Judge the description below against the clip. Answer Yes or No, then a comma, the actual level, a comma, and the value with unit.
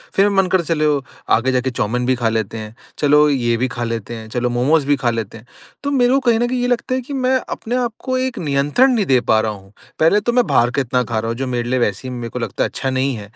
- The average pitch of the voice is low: Yes, low, 130 Hz